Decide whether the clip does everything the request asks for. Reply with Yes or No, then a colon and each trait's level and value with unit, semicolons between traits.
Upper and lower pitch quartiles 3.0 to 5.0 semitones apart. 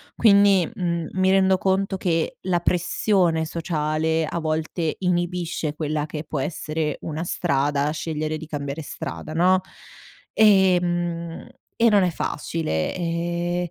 No: narrow, 2.6 semitones